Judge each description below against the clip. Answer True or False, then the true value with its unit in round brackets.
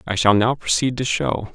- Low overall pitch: True (115 Hz)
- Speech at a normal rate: False (230 wpm)